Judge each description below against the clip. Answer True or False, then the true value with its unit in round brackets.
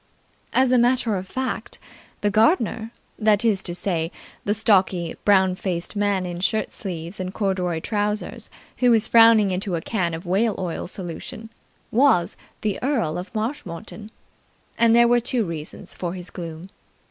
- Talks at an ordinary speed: True (160 wpm)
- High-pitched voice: True (200 Hz)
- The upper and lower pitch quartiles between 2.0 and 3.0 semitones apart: False (4.0 semitones)